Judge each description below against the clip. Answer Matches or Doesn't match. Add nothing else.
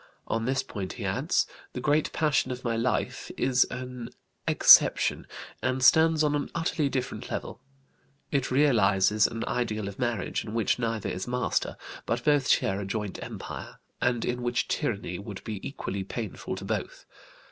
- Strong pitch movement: Doesn't match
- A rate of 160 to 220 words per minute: Matches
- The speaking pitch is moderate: Doesn't match